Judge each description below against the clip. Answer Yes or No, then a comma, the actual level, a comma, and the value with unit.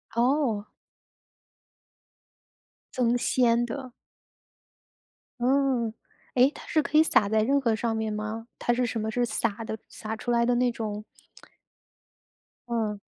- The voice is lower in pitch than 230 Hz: No, high, 235 Hz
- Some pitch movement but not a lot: No, narrow, 2.3 semitones